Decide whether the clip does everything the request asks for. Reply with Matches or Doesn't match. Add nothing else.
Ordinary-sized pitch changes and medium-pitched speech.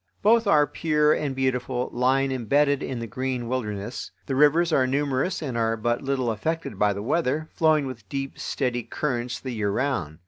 Doesn't match